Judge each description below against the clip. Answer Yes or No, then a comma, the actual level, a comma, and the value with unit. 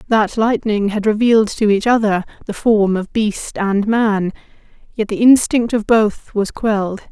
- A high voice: Yes, high, 215 Hz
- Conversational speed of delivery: Yes, average, 170 wpm